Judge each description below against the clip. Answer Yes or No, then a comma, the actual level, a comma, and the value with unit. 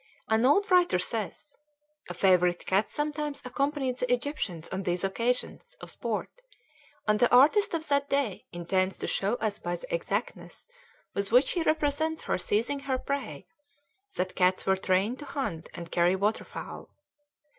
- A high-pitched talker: Yes, high, 230 Hz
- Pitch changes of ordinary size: No, wide, 7.2 semitones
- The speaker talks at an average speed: Yes, average, 160 wpm